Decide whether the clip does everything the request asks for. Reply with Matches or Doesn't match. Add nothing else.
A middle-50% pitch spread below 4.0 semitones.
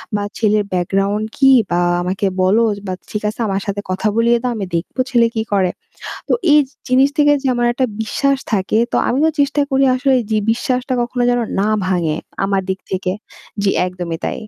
Doesn't match